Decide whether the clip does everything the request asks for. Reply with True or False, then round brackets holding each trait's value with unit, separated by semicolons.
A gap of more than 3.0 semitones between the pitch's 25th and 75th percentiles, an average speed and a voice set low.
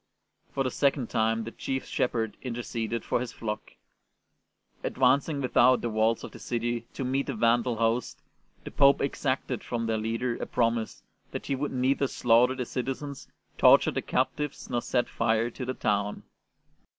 False (2.4 semitones; 165 wpm; 120 Hz)